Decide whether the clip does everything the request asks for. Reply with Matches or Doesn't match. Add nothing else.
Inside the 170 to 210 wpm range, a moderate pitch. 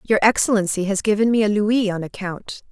Doesn't match